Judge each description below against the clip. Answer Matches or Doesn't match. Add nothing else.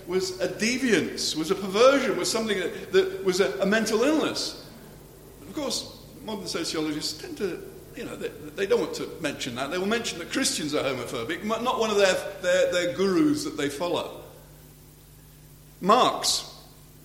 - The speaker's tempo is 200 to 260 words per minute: Doesn't match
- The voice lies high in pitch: Matches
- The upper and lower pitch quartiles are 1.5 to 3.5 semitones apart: Doesn't match